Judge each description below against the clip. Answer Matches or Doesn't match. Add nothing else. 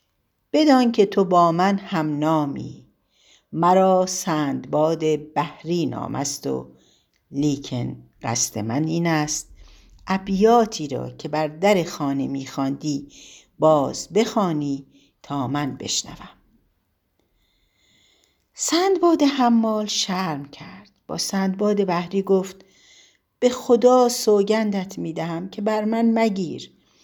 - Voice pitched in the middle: Matches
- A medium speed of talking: Doesn't match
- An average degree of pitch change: Doesn't match